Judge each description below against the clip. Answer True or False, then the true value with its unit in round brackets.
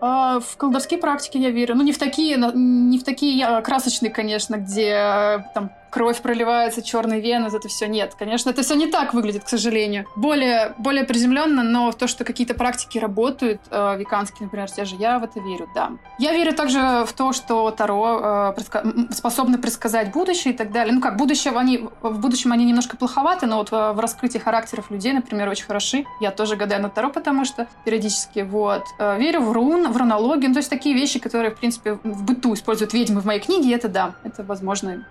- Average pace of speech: False (205 wpm)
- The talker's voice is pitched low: False (235 Hz)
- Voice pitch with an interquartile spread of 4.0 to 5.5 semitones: False (3.3 semitones)